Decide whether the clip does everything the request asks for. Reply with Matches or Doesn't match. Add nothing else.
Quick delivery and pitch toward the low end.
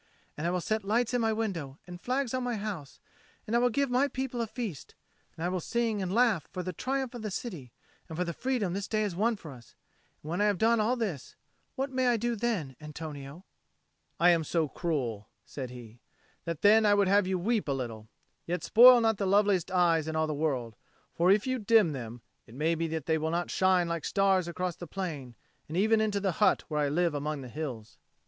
Doesn't match